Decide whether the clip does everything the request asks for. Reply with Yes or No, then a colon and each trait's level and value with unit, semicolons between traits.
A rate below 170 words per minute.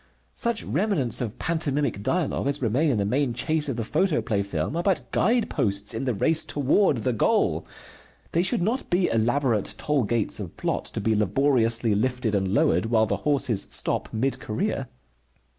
No: average, 175 wpm